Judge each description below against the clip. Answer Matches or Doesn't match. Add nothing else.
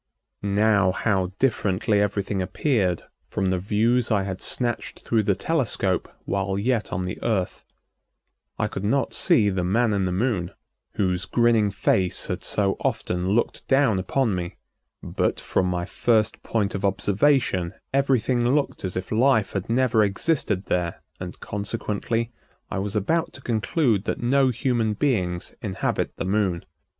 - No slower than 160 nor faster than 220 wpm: Doesn't match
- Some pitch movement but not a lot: Matches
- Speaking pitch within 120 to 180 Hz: Doesn't match